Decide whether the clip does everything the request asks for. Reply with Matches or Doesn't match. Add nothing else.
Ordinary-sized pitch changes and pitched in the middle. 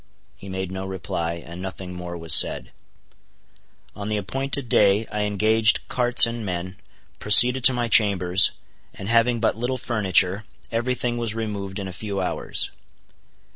Doesn't match